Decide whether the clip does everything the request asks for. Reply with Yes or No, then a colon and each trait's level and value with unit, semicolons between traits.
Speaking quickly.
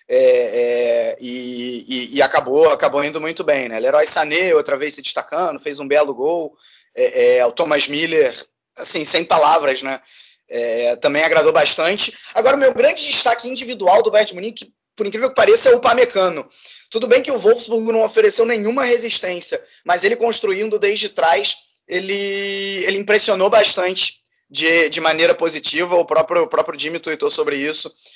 No: average, 170 wpm